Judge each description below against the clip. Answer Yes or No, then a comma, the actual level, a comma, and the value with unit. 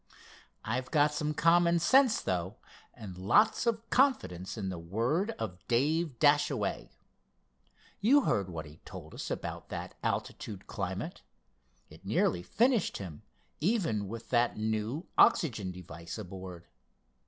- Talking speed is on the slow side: Yes, slow, 130 wpm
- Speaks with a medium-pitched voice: No, low, 115 Hz